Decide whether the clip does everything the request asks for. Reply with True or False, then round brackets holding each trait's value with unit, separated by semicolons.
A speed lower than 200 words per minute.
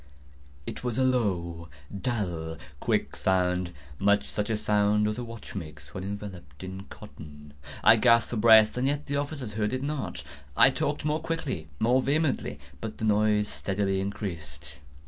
True (150 wpm)